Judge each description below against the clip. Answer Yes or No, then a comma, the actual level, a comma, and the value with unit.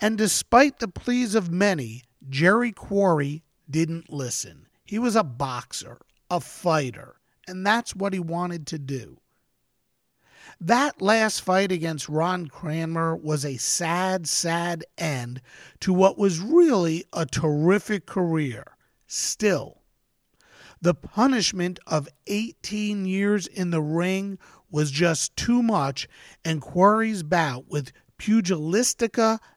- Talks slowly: Yes, slow, 120 wpm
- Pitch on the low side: No, medium, 175 Hz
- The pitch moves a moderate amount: Yes, average, 4.9 semitones